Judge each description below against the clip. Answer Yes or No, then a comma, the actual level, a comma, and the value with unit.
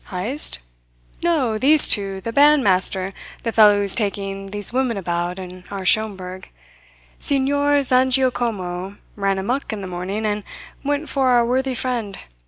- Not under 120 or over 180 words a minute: Yes, average, 140 wpm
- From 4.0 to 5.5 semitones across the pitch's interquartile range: Yes, average, 5.2 semitones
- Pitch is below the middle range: No, high, 215 Hz